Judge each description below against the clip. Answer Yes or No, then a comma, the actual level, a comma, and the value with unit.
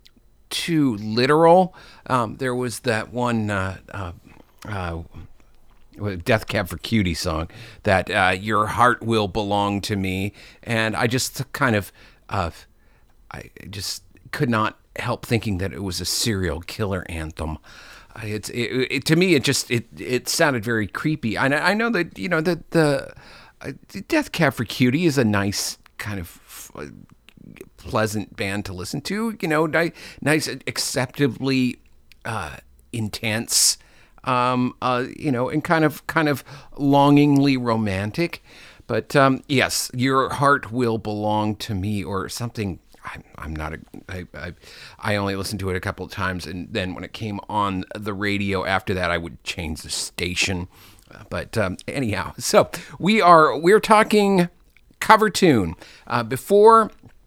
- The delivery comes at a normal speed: Yes, average, 155 wpm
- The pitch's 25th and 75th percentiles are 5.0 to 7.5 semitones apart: Yes, wide, 5.5 semitones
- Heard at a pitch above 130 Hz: No, low, 110 Hz